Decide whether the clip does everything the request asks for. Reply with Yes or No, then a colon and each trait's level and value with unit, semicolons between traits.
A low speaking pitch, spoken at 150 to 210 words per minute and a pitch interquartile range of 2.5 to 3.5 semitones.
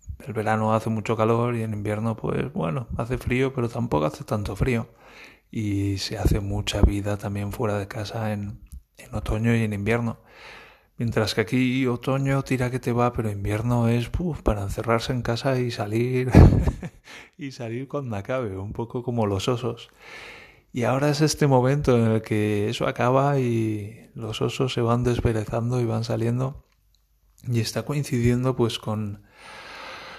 Yes: low, 115 Hz; average, 165 wpm; average, 2.9 semitones